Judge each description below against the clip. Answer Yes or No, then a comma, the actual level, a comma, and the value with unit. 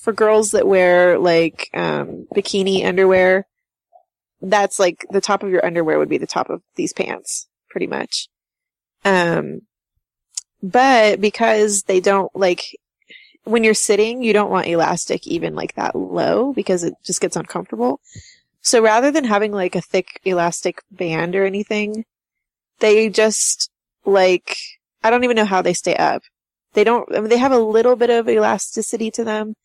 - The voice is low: No, high, 210 Hz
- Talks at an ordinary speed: Yes, average, 165 wpm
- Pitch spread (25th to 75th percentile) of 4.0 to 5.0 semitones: No, average, 3.0 semitones